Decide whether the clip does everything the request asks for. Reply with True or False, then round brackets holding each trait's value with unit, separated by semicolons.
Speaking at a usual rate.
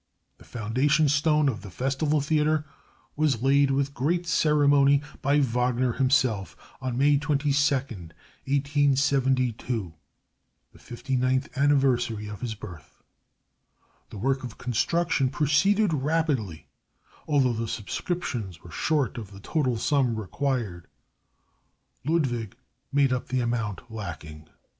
False (115 wpm)